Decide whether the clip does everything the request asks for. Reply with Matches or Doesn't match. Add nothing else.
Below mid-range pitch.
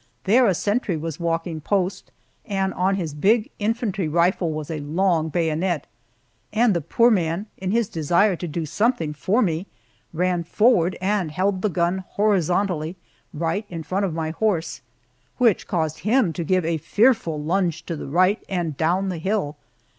Doesn't match